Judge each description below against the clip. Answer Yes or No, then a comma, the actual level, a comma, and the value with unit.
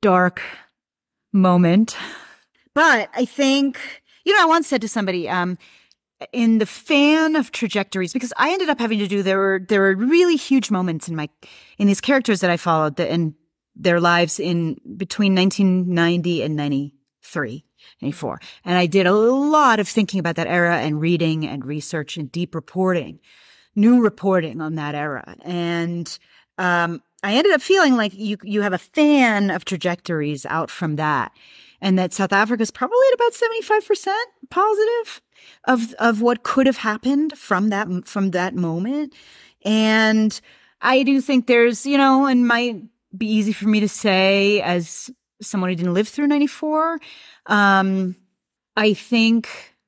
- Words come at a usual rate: Yes, average, 165 wpm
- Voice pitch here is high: Yes, high, 205 Hz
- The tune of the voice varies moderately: No, wide, 6.4 semitones